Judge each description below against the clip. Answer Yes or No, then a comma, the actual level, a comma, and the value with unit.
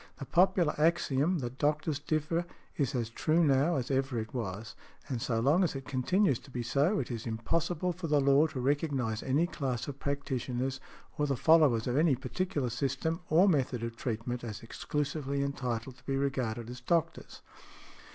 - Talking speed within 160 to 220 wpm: Yes, average, 180 wpm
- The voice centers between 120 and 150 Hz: Yes, medium, 140 Hz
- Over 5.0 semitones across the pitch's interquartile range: No, average, 4.0 semitones